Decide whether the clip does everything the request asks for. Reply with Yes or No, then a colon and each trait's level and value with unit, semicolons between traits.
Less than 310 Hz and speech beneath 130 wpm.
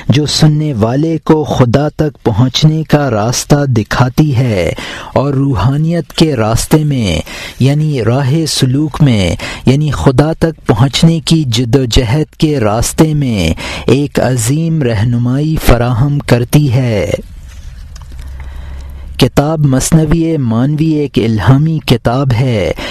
Yes: low, 135 Hz; average, 115 wpm